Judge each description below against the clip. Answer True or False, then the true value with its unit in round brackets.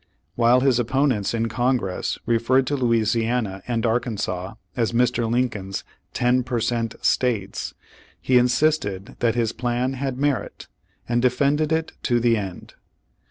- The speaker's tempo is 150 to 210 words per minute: False (135 wpm)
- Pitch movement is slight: True (2.1 semitones)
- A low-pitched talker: True (120 Hz)